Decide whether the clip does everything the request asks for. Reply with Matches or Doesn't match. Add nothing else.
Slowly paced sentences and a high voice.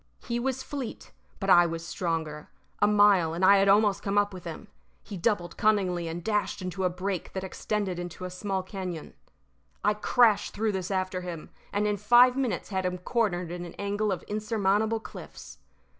Doesn't match